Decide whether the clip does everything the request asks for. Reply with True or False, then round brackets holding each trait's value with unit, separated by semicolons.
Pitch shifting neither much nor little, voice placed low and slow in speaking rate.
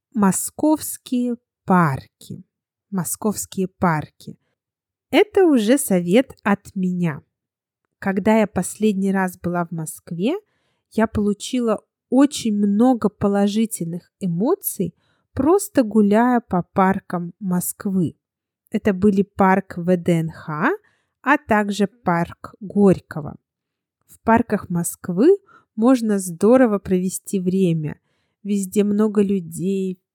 False (3.8 semitones; 200 Hz; 90 wpm)